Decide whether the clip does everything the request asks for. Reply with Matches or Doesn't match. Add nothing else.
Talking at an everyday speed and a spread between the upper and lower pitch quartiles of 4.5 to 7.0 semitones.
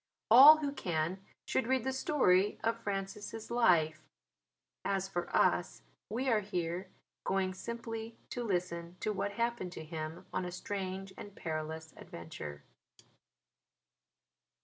Doesn't match